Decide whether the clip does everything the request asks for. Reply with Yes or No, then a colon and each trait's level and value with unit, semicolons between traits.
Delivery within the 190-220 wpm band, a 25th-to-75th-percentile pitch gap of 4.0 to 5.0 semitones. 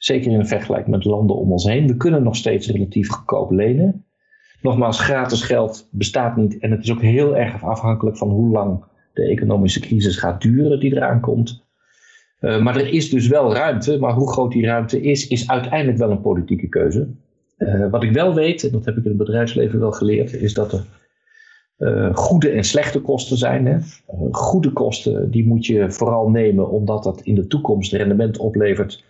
Yes: average, 195 wpm; average, 4.6 semitones